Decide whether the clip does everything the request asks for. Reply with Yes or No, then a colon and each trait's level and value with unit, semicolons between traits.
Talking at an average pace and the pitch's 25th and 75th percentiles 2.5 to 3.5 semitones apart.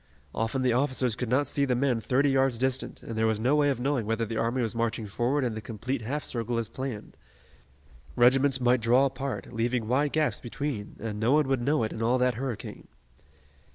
No: fast, 215 wpm; average, 2.9 semitones